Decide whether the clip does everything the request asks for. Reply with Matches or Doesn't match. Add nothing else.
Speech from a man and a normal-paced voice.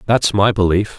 Matches